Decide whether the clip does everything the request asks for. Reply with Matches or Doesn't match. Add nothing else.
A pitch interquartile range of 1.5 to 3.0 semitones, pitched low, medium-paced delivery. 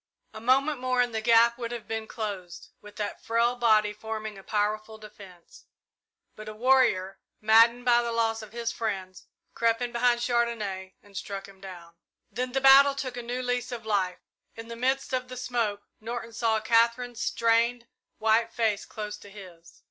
Doesn't match